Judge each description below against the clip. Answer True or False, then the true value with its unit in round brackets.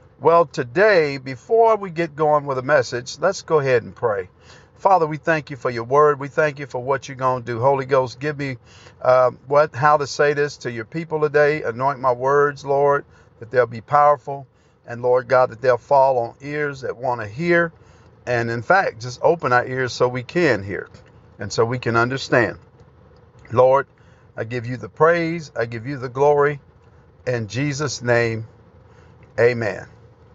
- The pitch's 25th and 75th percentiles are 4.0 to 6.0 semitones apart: False (3.4 semitones)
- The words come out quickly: False (190 wpm)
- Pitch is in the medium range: False (130 Hz)